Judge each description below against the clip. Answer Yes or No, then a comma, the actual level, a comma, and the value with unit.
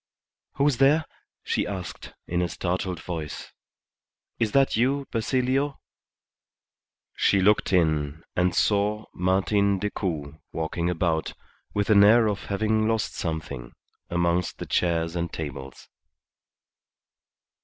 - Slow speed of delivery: Yes, slow, 110 wpm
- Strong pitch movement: No, average, 4.6 semitones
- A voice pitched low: Yes, very low, 95 Hz